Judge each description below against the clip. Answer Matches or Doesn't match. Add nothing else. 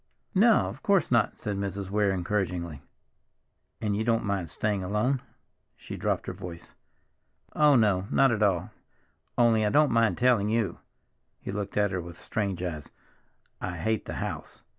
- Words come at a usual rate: Matches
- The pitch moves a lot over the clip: Doesn't match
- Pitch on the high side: Doesn't match